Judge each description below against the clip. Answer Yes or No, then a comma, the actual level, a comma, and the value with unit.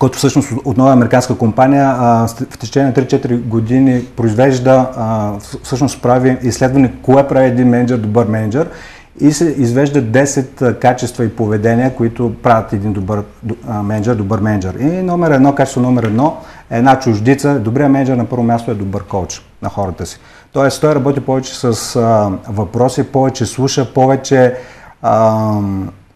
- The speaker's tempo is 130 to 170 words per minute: Yes, average, 160 wpm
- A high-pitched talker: No, low, 125 Hz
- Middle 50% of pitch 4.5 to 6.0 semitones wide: No, average, 3.2 semitones